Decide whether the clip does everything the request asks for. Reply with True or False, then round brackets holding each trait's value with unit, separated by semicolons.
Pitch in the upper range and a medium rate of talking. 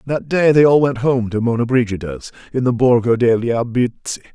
False (120 Hz; 195 wpm)